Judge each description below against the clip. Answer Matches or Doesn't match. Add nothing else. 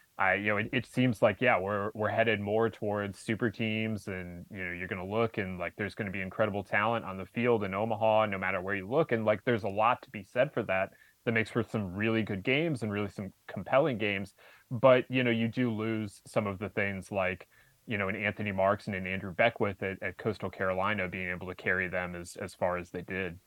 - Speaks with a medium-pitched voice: Doesn't match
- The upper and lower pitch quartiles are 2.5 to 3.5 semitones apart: Matches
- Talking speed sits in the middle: Doesn't match